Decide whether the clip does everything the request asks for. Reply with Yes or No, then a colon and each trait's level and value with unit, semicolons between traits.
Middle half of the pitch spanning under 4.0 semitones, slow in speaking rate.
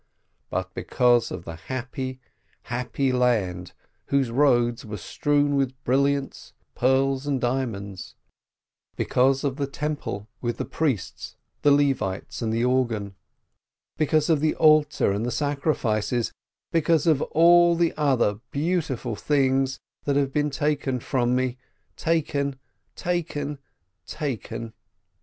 Yes: average, 3.4 semitones; slow, 120 wpm